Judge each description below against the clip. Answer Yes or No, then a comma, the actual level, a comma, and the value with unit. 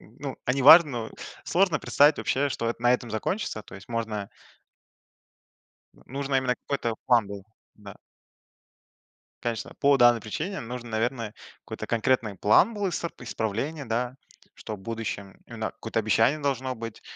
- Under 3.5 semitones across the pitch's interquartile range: No, average, 3.9 semitones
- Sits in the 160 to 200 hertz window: No, low, 120 Hz